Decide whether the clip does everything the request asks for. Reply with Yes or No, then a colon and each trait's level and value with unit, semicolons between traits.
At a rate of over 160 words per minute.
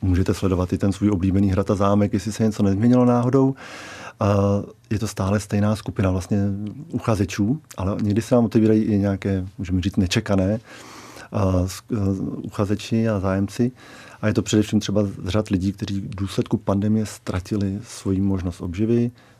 No: average, 150 wpm